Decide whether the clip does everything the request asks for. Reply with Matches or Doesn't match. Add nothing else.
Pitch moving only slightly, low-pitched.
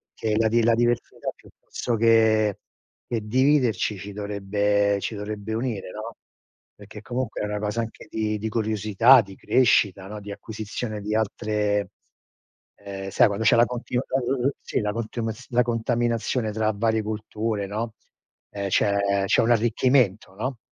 Matches